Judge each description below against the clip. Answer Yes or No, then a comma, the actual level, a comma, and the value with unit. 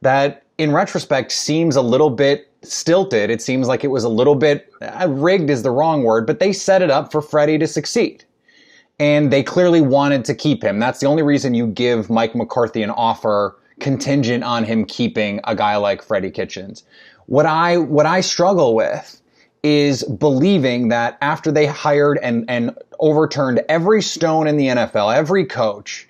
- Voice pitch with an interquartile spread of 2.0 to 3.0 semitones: No, average, 3.7 semitones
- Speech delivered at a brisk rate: No, average, 180 wpm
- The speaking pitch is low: No, medium, 145 Hz